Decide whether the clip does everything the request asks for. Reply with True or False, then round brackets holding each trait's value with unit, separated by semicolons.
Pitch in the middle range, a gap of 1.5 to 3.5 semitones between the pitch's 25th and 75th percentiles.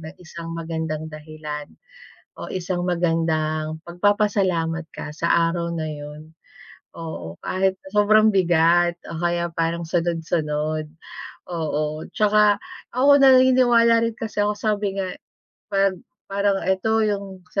False (175 Hz; 4.1 semitones)